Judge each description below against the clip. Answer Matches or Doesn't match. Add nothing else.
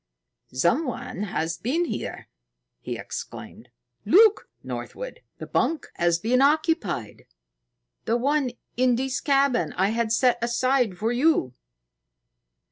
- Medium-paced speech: Doesn't match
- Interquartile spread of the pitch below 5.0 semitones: Doesn't match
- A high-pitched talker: Matches